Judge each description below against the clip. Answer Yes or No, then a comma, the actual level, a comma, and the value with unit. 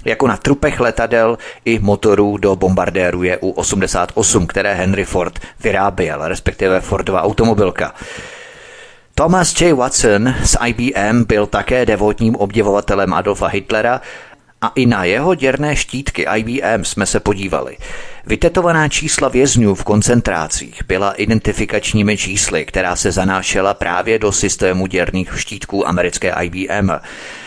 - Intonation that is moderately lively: Yes, average, 4.8 semitones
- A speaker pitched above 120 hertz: No, low, 105 Hz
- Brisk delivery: No, average, 120 wpm